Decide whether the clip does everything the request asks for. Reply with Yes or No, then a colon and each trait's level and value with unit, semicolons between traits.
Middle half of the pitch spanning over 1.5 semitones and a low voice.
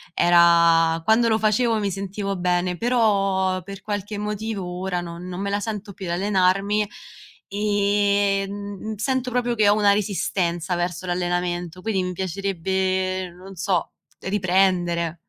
No: narrow, 2.4 semitones; high, 195 Hz